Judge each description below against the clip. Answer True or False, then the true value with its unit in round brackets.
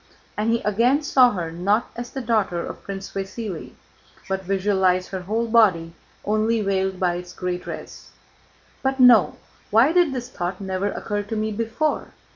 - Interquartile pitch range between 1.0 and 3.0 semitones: False (3.6 semitones)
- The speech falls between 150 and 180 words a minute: True (165 wpm)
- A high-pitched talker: True (205 Hz)